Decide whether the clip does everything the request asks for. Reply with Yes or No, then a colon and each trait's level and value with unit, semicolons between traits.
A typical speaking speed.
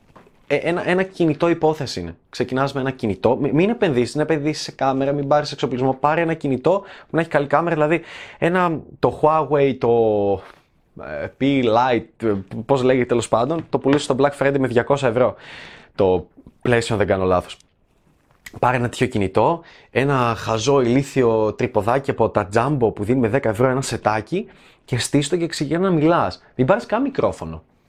No: fast, 175 wpm